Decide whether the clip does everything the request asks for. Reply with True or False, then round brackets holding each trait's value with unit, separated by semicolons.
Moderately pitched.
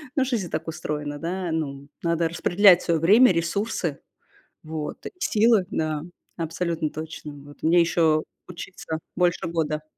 True (165 Hz)